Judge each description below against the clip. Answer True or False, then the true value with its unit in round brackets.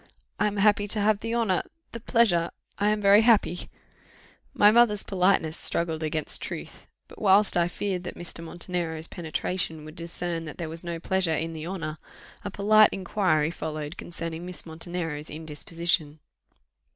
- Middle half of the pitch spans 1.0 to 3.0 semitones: False (3.9 semitones)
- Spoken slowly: False (165 wpm)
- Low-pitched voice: False (175 Hz)